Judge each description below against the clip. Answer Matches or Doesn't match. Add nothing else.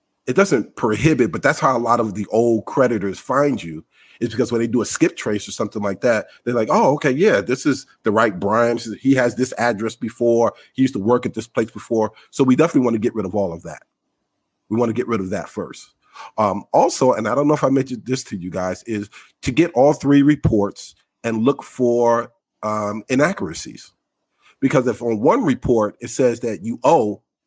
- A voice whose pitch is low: Matches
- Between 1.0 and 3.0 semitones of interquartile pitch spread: Matches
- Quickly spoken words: Matches